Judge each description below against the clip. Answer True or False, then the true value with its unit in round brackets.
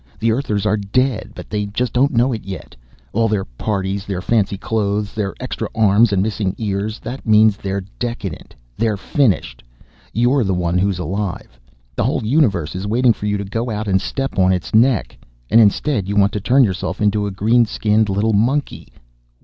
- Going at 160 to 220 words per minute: True (190 wpm)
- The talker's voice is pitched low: True (105 Hz)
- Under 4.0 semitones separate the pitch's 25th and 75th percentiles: True (2.8 semitones)